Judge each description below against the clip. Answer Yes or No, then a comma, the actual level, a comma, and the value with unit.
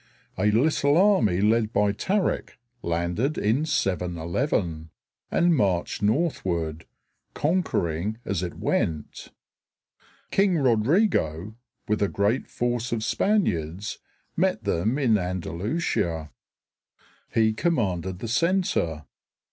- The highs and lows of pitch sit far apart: Yes, wide, 8.5 semitones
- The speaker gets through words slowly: Yes, slow, 100 wpm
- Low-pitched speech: Yes, low, 105 Hz